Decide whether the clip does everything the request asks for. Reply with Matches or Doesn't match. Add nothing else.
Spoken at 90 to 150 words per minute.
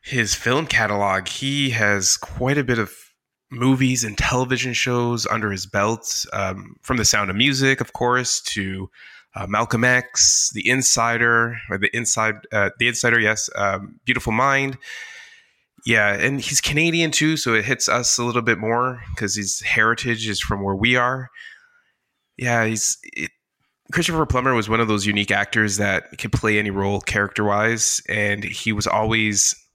Doesn't match